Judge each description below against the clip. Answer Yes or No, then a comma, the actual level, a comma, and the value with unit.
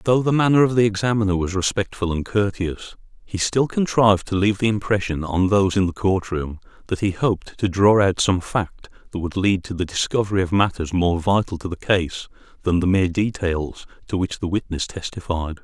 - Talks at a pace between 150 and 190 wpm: No, fast, 205 wpm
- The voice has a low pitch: Yes, very low, 95 Hz